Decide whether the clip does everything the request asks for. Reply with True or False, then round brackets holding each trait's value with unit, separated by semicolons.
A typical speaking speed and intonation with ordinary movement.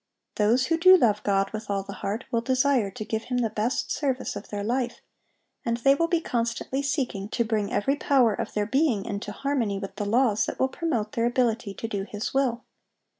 False (215 wpm; 4.2 semitones)